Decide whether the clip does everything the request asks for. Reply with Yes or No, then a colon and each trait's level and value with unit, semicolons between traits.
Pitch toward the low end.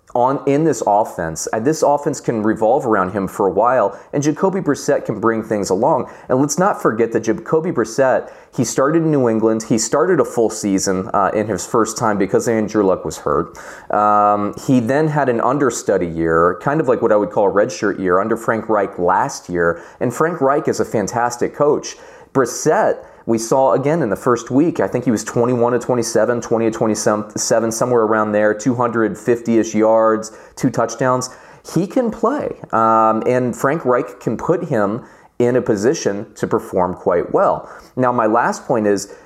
Yes: low, 115 Hz